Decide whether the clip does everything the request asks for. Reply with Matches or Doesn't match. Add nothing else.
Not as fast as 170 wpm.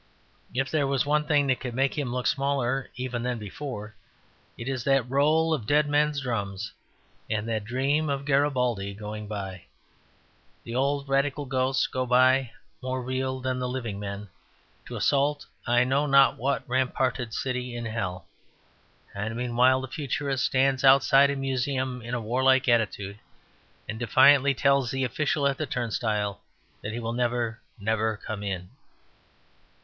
Matches